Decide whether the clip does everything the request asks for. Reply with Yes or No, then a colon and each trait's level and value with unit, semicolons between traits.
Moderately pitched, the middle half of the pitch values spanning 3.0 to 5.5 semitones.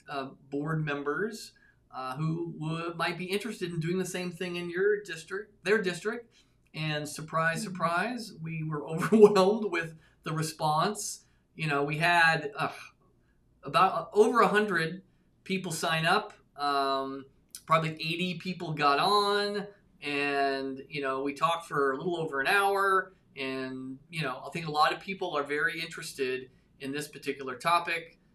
Yes: medium, 165 Hz; average, 4.4 semitones